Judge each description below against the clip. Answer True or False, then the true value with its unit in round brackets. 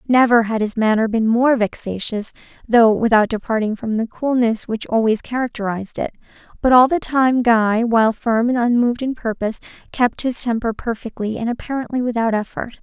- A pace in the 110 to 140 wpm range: False (170 wpm)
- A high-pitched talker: True (230 Hz)